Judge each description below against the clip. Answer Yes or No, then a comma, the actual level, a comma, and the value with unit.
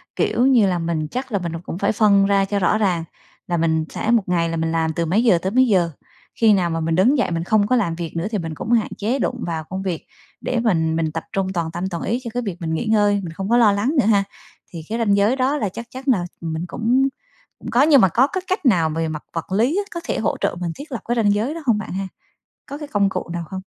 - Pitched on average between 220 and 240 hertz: No, high, 200 Hz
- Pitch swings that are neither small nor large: No, wide, 5.7 semitones